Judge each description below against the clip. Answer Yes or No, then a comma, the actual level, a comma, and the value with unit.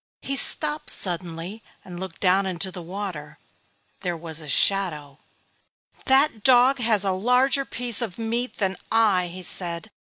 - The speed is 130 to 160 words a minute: Yes, average, 150 wpm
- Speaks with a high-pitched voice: Yes, high, 195 Hz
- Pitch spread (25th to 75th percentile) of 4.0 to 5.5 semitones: Yes, average, 5.2 semitones